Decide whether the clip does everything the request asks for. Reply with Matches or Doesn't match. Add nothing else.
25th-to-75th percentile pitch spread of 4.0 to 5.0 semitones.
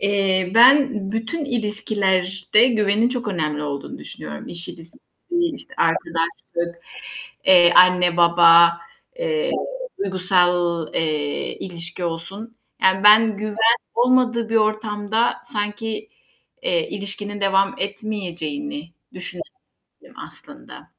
Matches